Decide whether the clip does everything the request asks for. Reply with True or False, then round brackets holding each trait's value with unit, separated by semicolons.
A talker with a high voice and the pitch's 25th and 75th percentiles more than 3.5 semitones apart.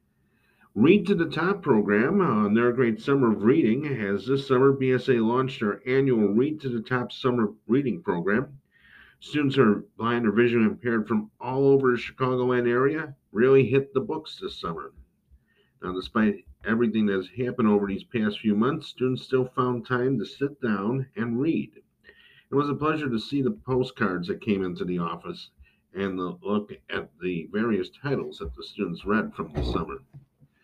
False (125 Hz; 4.1 semitones)